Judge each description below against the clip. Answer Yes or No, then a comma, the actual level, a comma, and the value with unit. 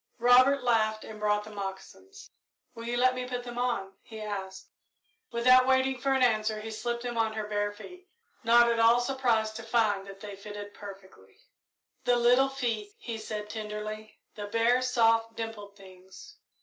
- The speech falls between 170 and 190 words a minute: Yes, average, 175 wpm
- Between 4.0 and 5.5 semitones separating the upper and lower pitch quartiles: No, average, 2.8 semitones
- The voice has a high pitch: Yes, high, 225 Hz